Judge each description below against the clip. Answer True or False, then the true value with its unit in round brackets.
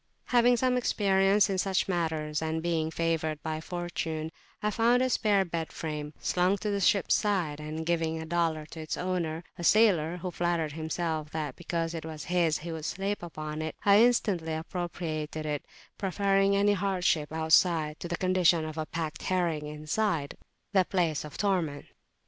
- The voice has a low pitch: False (170 Hz)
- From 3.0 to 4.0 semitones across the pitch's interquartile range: True (3.4 semitones)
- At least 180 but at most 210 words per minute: False (170 wpm)